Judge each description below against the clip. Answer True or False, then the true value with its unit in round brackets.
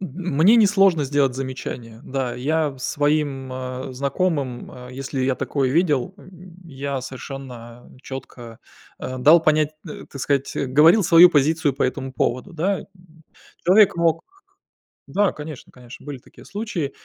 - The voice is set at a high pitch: False (140 Hz)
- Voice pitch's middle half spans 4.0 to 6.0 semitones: True (4.3 semitones)